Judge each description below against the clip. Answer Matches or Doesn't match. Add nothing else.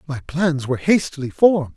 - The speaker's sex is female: Doesn't match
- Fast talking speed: Doesn't match